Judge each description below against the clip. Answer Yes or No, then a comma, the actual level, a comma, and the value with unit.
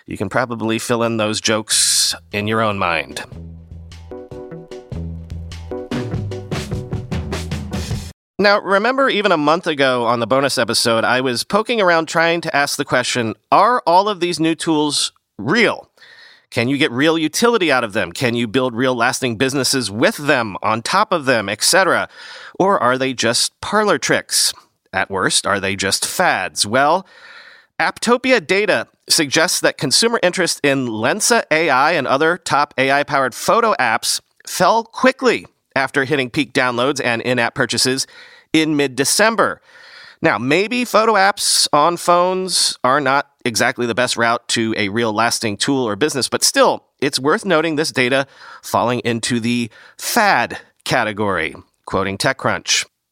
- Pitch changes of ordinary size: No, wide, 6.3 semitones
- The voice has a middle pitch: No, low, 130 Hz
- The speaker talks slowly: No, average, 150 wpm